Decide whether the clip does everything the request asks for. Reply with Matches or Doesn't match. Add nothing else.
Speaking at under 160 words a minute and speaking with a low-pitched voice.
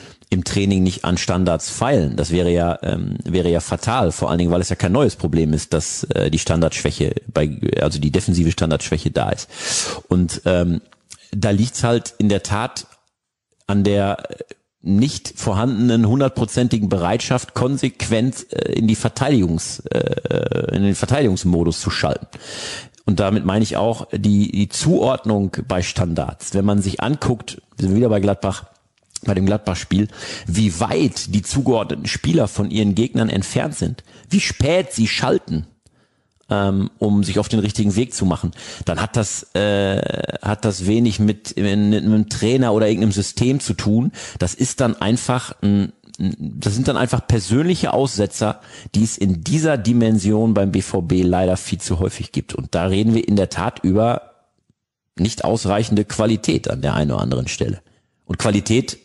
Doesn't match